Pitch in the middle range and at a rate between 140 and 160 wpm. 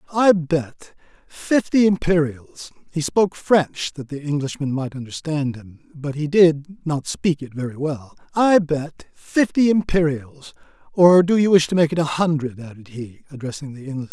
Yes: medium, 150 Hz; average, 155 wpm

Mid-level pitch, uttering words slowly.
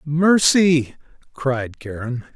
Yes: medium, 145 Hz; slow, 75 wpm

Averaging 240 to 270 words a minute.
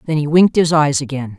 Yes: fast, 260 wpm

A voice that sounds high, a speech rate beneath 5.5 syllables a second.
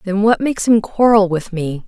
Yes: high, 200 Hz; 5.1 syllables/s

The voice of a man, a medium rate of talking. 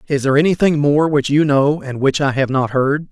No: male; fast, 250 wpm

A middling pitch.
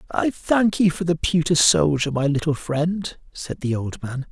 Yes: medium, 160 Hz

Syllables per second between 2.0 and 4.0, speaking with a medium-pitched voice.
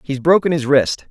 No: 5.1 syllables/s; medium, 145 Hz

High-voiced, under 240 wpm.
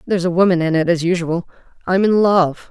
No: medium, 175 Hz; average, 200 wpm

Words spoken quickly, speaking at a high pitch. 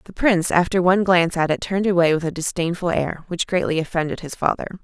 No: fast, 225 wpm; medium, 175 Hz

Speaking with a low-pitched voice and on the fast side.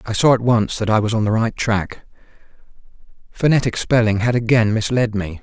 No: low, 110 Hz; average, 190 wpm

